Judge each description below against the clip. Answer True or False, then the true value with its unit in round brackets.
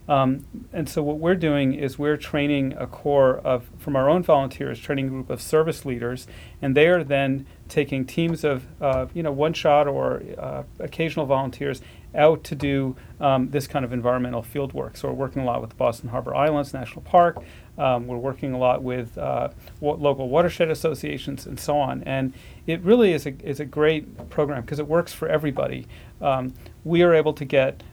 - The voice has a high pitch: False (140 Hz)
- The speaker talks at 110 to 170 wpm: False (200 wpm)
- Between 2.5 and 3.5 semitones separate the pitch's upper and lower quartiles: True (3.0 semitones)